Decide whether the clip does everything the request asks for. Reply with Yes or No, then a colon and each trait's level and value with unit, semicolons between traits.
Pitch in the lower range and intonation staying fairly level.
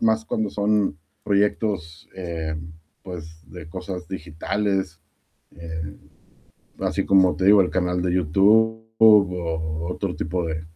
No: very low, 90 Hz; average, 3.8 semitones